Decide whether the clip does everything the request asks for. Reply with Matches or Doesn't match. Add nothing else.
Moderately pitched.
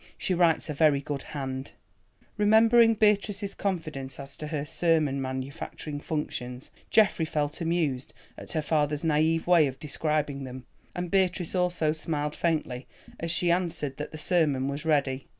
Matches